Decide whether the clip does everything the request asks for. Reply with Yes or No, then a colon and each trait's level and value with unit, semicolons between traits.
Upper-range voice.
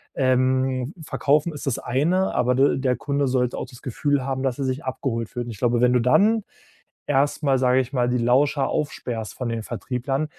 No: low, 130 Hz